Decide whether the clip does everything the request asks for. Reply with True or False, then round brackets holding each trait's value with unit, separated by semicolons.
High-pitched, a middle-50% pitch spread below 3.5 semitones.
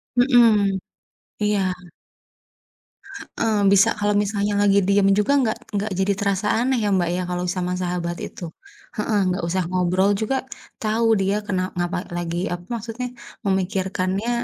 True (200 Hz; 2.7 semitones)